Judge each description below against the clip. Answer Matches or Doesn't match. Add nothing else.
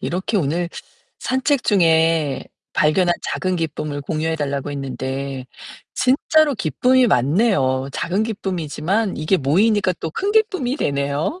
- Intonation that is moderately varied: Doesn't match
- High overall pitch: Doesn't match